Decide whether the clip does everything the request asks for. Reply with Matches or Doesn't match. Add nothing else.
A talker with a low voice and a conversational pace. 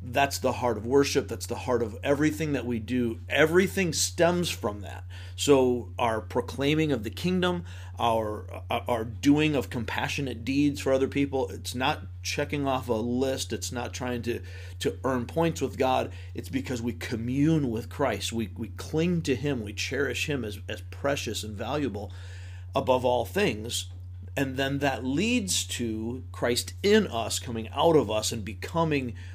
Matches